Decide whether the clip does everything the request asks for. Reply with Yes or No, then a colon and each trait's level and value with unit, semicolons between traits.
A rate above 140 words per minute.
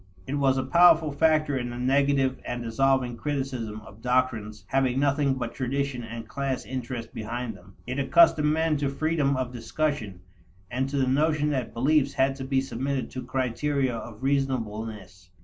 Yes: average, 165 wpm